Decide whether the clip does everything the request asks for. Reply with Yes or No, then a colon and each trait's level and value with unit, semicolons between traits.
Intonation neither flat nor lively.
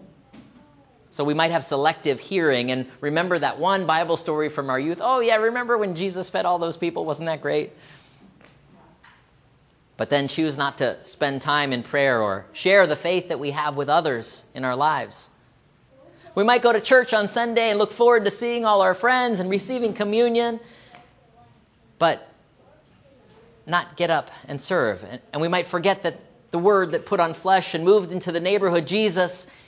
No: wide, 5.9 semitones